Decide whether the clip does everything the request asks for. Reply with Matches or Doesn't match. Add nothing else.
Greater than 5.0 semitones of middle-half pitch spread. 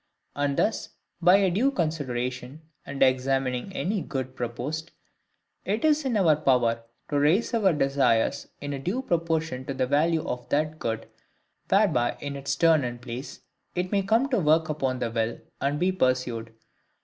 Matches